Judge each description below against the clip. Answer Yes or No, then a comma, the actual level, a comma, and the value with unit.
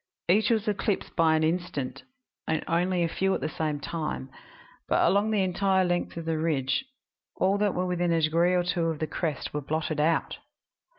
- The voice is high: No, medium, 170 Hz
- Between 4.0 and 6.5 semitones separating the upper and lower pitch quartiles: No, average, 2.9 semitones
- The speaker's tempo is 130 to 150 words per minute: No, average, 195 wpm